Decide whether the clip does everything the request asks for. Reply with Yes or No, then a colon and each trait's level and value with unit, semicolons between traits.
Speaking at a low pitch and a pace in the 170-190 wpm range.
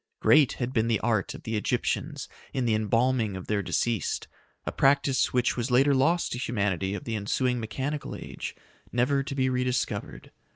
Yes: low, 120 Hz; average, 175 wpm